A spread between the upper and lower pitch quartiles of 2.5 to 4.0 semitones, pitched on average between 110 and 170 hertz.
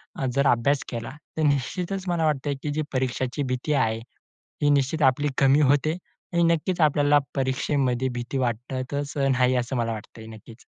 Yes: average, 2.9 semitones; low, 135 Hz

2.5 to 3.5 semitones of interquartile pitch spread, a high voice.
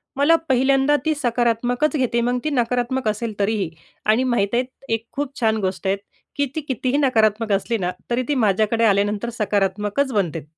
No: average, 3.9 semitones; high, 235 Hz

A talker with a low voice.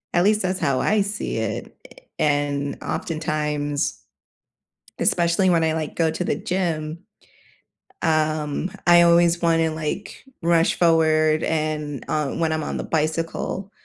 No: medium, 160 Hz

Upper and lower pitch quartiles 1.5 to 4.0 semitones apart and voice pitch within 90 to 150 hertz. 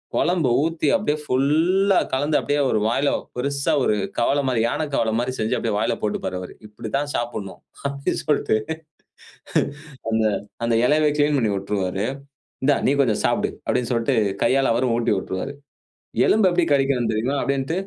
No: average, 4.5 semitones; low, 135 Hz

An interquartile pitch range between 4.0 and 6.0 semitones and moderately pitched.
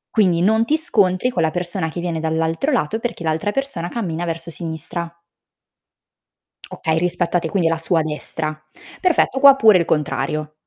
Yes: average, 5.2 semitones; medium, 175 Hz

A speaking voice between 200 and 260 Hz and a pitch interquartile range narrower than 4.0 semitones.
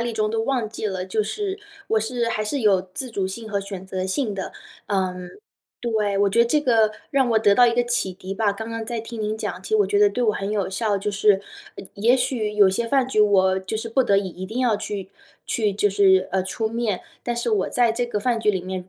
Yes: high, 215 Hz; average, 3.2 semitones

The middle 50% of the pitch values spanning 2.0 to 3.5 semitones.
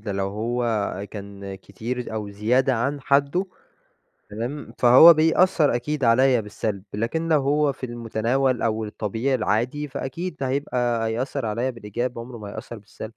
No: average, 3.9 semitones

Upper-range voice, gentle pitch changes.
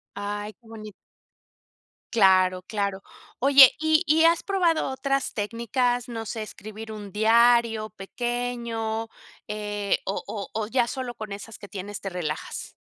No: high, 225 Hz; average, 3.0 semitones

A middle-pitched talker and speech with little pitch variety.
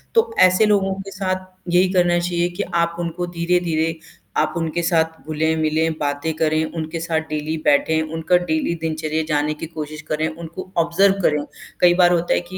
Yes: medium, 165 Hz; narrow, 2.0 semitones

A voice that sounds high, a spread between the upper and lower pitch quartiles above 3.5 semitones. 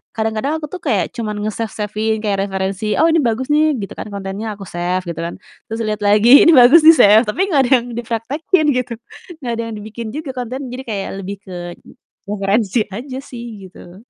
Yes: high, 220 Hz; average, 4.1 semitones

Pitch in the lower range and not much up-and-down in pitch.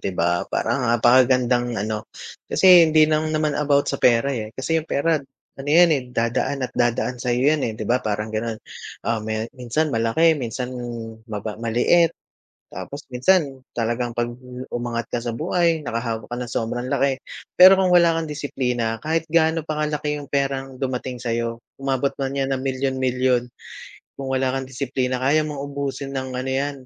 No: low, 130 Hz; average, 3.6 semitones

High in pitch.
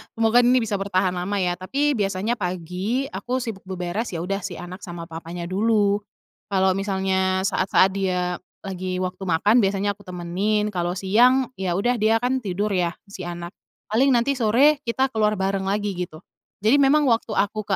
Yes: high, 195 Hz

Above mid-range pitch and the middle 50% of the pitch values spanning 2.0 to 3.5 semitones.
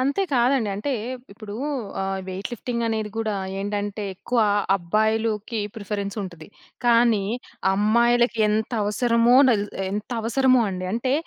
Yes: high, 220 Hz; average, 2.7 semitones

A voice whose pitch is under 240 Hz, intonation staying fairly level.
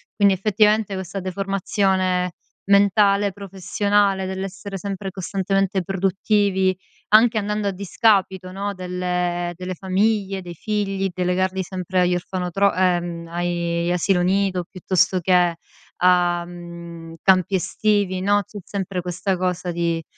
Yes: high, 190 Hz; narrow, 1.9 semitones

